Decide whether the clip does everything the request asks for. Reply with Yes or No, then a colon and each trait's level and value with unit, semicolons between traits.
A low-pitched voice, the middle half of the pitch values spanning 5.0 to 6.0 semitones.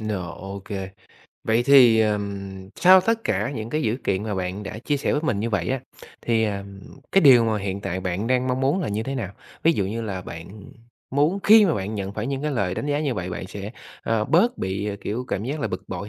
Yes: low, 110 Hz; wide, 5.5 semitones